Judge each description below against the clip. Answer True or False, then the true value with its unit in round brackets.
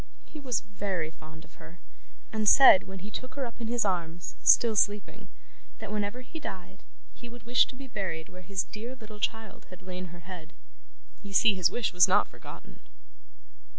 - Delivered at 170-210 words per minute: True (190 wpm)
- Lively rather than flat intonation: False (4.3 semitones)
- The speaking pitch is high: True (205 Hz)